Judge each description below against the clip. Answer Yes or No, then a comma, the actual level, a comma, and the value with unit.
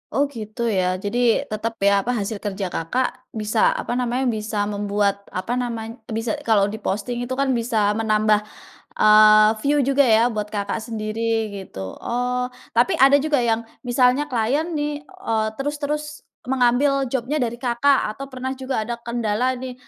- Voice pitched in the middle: No, high, 235 Hz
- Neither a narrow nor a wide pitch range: Yes, average, 3.4 semitones